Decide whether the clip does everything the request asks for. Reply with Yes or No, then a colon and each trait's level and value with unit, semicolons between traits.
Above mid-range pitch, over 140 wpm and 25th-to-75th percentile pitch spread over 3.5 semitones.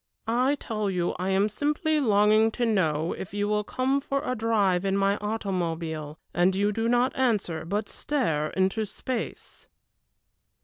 Yes: high, 210 Hz; average, 160 wpm; average, 4.0 semitones